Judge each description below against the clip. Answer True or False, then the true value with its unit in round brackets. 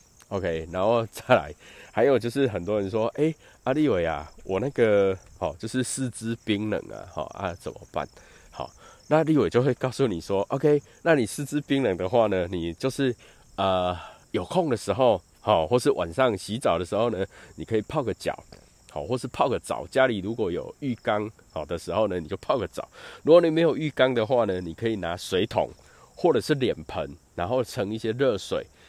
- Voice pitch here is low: True (115 Hz)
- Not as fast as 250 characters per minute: False (290 characters per minute)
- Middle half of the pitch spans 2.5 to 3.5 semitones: False (5.2 semitones)